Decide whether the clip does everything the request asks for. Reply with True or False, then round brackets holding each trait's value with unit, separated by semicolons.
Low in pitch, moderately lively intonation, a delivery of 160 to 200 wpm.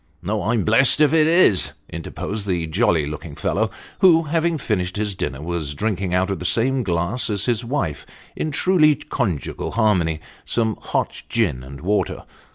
False (105 Hz; 6.6 semitones; 170 wpm)